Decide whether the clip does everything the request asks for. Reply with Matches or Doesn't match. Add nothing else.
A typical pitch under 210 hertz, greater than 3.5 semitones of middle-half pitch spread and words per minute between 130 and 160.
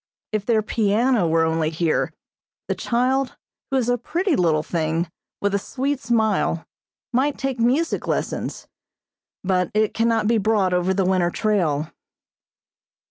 Doesn't match